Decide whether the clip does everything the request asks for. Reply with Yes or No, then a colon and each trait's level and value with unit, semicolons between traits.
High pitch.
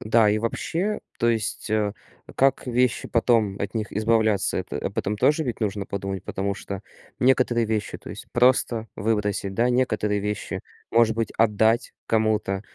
No: low, 110 Hz